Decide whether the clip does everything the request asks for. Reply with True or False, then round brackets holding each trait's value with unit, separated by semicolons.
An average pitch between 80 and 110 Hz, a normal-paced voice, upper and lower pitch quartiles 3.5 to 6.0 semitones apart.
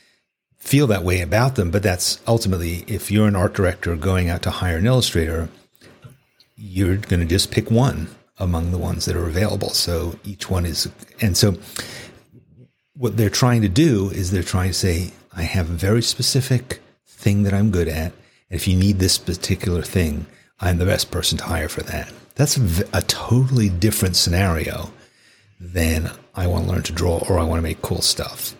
True (95 Hz; 190 wpm; 4.4 semitones)